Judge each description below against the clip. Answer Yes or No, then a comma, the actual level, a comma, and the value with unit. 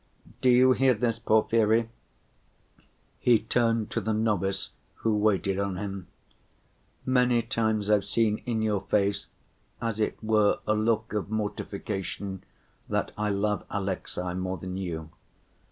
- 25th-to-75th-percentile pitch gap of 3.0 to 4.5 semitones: No, narrow, 2.5 semitones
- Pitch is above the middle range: No, low, 105 Hz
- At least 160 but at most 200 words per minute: No, slow, 135 wpm